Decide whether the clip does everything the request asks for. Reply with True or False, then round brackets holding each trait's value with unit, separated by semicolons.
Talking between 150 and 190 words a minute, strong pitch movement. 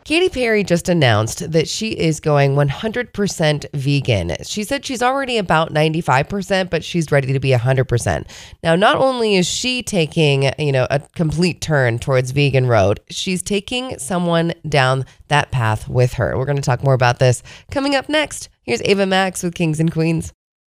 True (175 wpm; 6.3 semitones)